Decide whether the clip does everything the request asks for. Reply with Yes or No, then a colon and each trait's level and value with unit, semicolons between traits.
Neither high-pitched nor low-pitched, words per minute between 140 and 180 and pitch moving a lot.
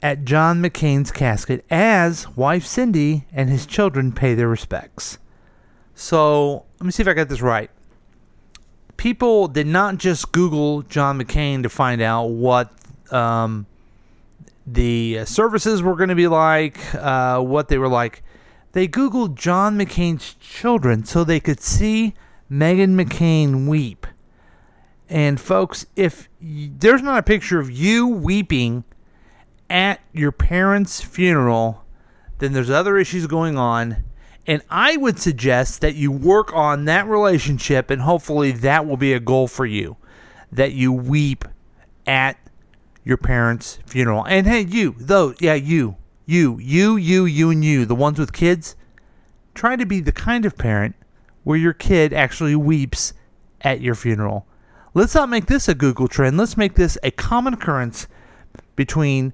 Yes: medium, 150 Hz; average, 155 wpm; wide, 6.3 semitones